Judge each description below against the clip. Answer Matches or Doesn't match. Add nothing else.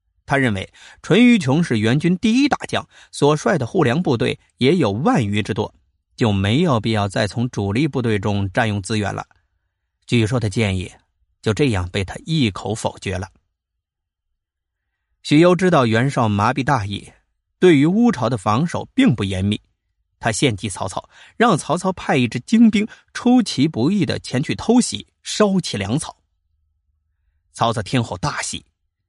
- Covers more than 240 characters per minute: Doesn't match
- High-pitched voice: Doesn't match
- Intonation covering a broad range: Matches